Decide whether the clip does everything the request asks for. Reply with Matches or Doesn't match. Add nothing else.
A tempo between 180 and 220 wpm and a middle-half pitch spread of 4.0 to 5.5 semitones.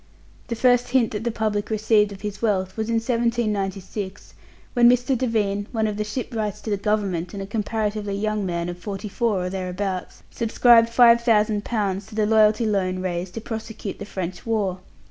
Doesn't match